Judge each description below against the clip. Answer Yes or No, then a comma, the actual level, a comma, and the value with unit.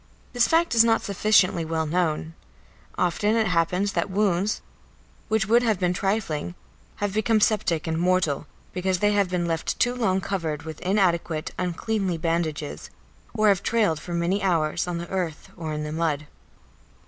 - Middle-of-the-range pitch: Yes, medium, 180 Hz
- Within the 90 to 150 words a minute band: No, average, 165 wpm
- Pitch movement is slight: No, average, 4.0 semitones